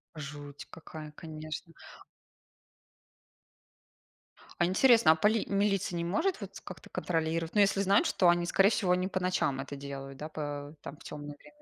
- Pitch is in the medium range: Yes, medium, 170 Hz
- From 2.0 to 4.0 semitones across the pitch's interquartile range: No, average, 4.7 semitones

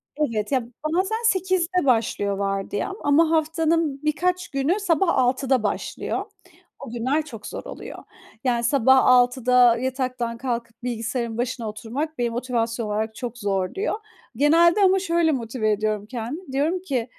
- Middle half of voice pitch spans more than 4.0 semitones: Yes, wide, 5.5 semitones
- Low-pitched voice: No, very high, 255 Hz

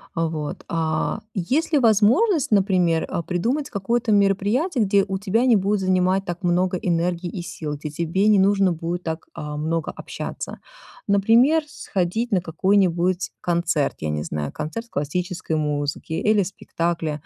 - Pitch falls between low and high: Yes, medium, 180 Hz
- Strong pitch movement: No, average, 3.8 semitones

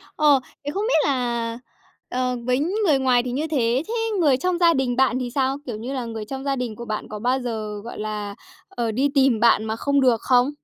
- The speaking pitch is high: Yes, very high, 250 Hz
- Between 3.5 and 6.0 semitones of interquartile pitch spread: No, average, 3.1 semitones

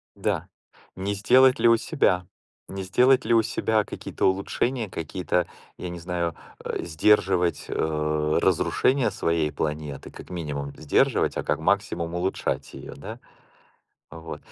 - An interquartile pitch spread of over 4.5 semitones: Yes, average, 4.9 semitones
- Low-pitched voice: Yes, very low, 90 Hz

